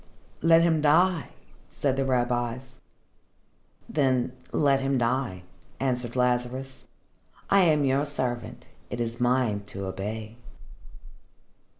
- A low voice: Yes, low, 130 Hz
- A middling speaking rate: No, slow, 105 wpm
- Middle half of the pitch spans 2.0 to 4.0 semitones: Yes, narrow, 2.5 semitones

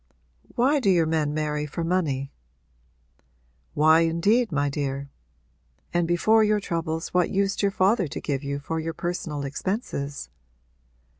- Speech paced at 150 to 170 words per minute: No, average, 140 wpm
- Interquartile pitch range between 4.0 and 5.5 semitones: Yes, average, 4.6 semitones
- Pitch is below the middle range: No, medium, 165 Hz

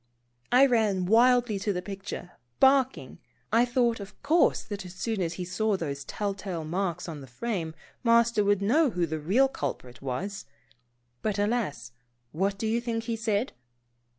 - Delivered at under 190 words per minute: Yes, average, 165 wpm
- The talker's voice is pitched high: Yes, high, 205 Hz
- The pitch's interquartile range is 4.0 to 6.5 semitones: Yes, average, 4.7 semitones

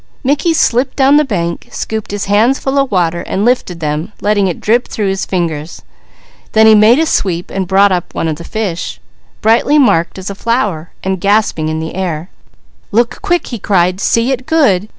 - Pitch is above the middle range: Yes, high, 200 Hz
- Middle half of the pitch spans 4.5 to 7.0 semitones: Yes, wide, 5.4 semitones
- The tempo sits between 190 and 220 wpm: Yes, average, 195 wpm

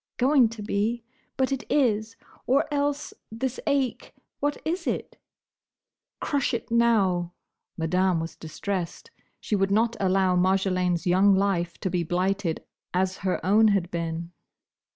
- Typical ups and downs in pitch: Yes, average, 4.6 semitones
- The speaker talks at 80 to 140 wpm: Yes, slow, 135 wpm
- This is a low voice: No, high, 195 Hz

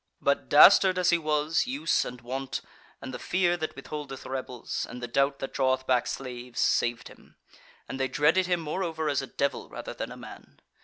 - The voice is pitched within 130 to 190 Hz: Yes, medium, 140 Hz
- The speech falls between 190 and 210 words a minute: Yes, average, 195 wpm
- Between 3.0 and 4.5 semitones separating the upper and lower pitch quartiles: Yes, average, 4.0 semitones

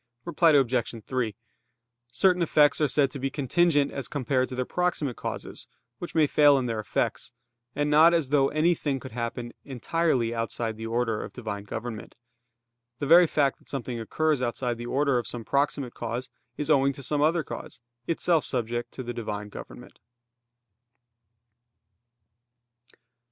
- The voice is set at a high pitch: No, low, 135 Hz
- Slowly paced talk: No, average, 155 wpm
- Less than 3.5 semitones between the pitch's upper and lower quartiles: No, average, 3.9 semitones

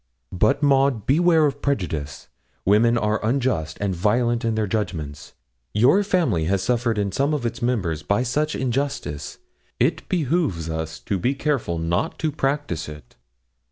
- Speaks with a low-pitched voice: Yes, low, 115 Hz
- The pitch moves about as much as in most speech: No, wide, 8.0 semitones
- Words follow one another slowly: No, average, 155 wpm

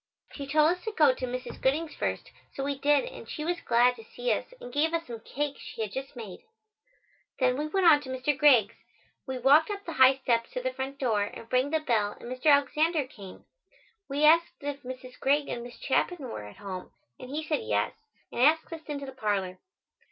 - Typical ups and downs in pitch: Yes, average, 3.7 semitones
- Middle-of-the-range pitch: No, very high, 270 Hz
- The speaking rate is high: Yes, fast, 220 wpm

